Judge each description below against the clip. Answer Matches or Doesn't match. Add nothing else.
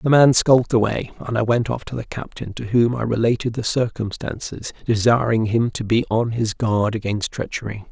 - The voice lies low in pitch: Matches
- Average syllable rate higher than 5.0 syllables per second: Matches